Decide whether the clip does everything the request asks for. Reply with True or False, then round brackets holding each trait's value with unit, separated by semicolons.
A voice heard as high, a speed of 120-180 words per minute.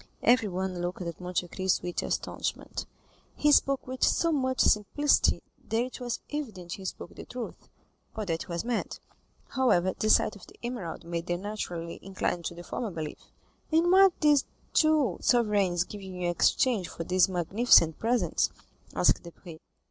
True (195 Hz; 170 wpm)